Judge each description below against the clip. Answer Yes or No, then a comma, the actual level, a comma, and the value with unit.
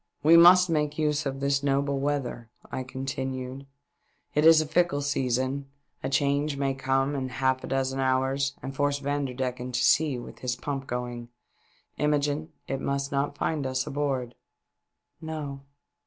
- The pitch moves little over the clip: Yes, narrow, 1.7 semitones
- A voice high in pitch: No, medium, 140 Hz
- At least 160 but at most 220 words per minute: Yes, average, 165 wpm